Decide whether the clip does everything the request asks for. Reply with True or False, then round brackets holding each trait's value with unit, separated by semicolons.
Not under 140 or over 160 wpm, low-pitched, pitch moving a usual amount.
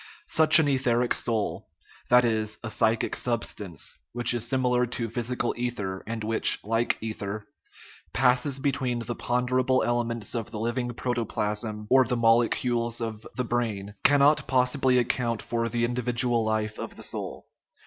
False (150 wpm; 120 Hz; 1.9 semitones)